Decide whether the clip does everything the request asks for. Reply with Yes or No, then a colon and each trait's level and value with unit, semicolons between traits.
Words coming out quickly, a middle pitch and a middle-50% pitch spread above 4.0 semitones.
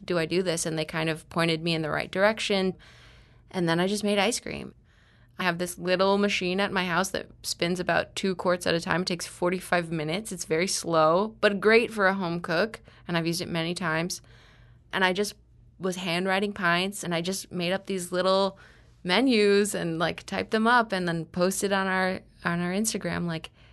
No: fast, 210 wpm; medium, 180 Hz; narrow, 2.6 semitones